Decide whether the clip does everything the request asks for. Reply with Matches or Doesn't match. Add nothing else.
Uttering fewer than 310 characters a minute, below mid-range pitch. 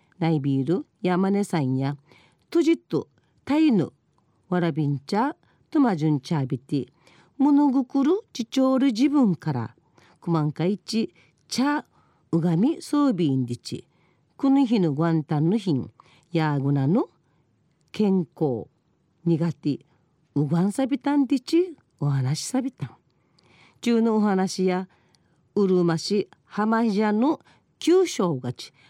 Doesn't match